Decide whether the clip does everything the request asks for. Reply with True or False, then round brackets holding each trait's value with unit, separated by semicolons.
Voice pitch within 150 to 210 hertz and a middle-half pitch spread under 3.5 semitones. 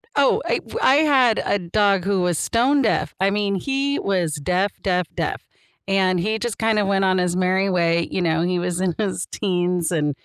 True (190 Hz; 3.0 semitones)